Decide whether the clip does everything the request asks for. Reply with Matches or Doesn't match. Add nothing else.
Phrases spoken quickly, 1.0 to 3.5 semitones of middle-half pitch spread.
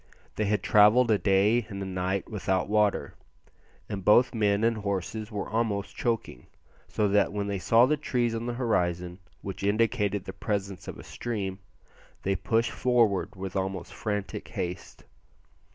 Doesn't match